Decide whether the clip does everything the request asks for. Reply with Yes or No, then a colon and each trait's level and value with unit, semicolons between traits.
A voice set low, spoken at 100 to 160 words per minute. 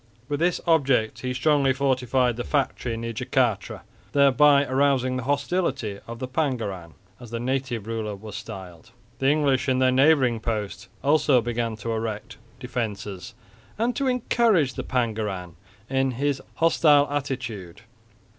Yes: low, 130 Hz; average, 140 wpm